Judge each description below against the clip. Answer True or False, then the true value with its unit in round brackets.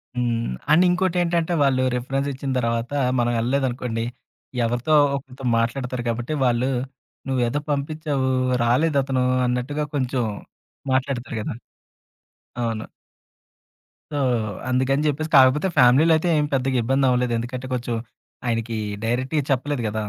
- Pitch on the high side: False (130 Hz)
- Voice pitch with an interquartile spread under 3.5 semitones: True (2.8 semitones)